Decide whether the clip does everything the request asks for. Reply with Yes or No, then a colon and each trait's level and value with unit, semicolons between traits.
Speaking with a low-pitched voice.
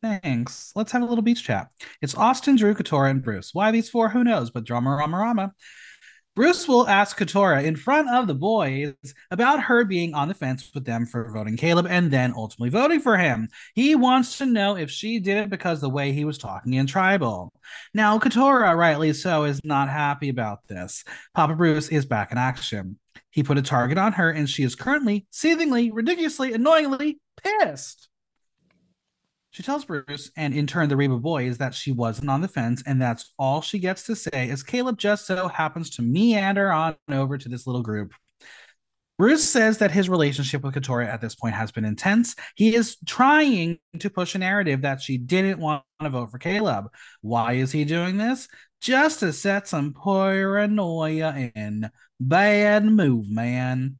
No: medium, 165 Hz